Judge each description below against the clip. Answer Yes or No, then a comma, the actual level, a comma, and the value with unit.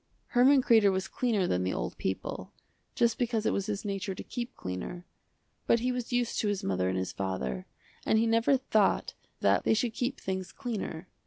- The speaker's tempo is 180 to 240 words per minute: Yes, average, 195 wpm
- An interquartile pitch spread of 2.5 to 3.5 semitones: No, average, 5.1 semitones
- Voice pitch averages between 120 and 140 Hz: No, high, 210 Hz